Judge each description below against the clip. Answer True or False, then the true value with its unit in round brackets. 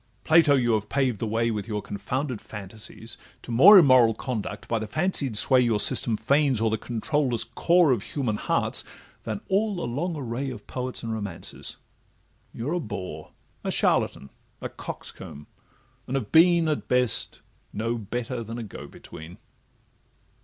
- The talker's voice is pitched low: True (120 Hz)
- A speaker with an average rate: True (155 wpm)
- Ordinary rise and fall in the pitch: True (4.4 semitones)